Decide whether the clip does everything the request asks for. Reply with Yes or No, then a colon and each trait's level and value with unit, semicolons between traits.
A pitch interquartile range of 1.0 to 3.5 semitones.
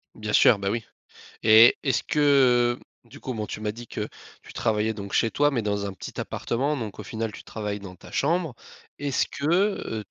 No: average, 4.0 semitones